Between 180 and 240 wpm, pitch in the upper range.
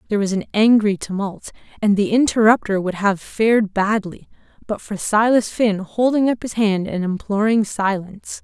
No: average, 165 wpm; high, 210 Hz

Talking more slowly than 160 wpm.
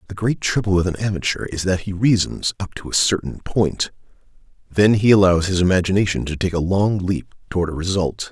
No: average, 200 wpm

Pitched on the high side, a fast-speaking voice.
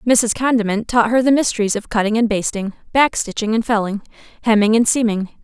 No: high, 220 Hz; average, 190 wpm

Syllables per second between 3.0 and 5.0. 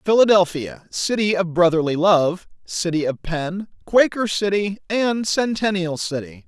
Yes: 4.3 syllables/s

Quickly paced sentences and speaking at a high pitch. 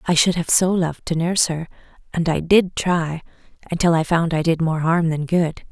No: fast, 220 wpm; medium, 165 Hz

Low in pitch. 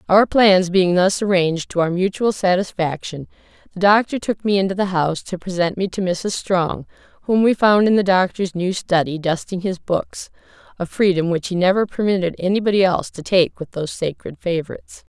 No: medium, 185 Hz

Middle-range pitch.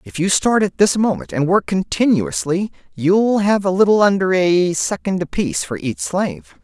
Yes: medium, 170 Hz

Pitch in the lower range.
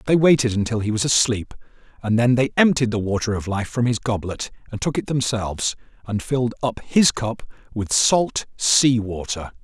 Yes: low, 115 Hz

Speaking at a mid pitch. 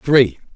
No: low, 125 Hz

